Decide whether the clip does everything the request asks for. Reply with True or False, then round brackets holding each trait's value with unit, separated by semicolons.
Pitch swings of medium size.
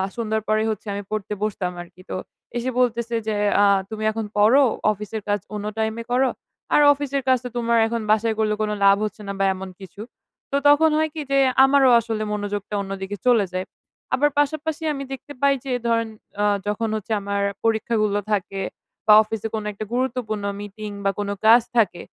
True (3.1 semitones)